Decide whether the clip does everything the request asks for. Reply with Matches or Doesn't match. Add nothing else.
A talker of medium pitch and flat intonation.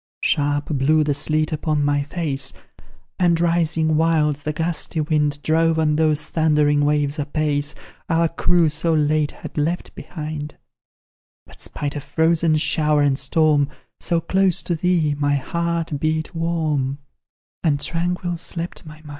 Matches